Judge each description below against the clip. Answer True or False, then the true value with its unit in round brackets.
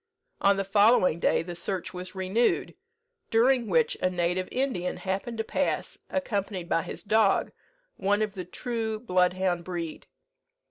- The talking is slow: False (145 wpm)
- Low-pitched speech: False (195 Hz)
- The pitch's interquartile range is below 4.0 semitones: True (3.6 semitones)